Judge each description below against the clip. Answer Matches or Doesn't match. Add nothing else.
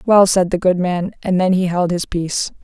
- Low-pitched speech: Doesn't match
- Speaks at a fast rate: Matches